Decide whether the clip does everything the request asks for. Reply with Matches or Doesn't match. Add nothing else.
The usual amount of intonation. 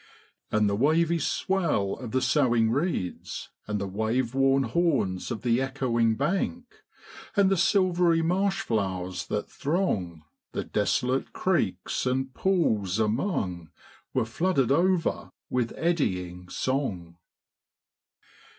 Doesn't match